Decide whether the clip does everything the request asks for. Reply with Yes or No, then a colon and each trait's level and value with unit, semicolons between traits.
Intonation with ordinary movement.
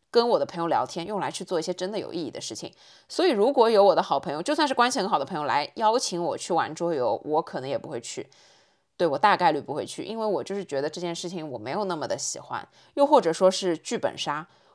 Yes: average, 5.0 semitones